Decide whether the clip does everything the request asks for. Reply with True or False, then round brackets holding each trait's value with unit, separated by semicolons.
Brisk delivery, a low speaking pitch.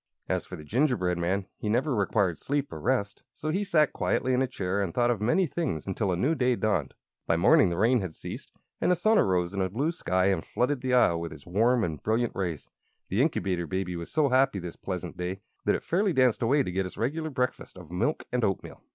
True (240 wpm; 110 Hz)